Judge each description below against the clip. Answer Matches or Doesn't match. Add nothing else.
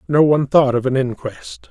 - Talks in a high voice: Doesn't match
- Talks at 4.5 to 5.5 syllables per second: Matches